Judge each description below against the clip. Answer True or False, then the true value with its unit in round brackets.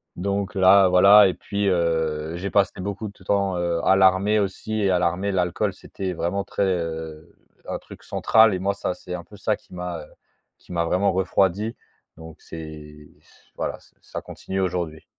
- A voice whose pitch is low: True (95 Hz)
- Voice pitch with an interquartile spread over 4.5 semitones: False (2.6 semitones)